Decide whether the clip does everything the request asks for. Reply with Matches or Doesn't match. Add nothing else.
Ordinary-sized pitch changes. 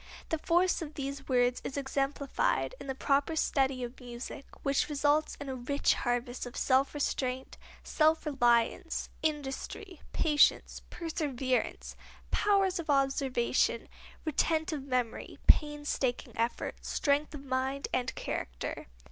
Matches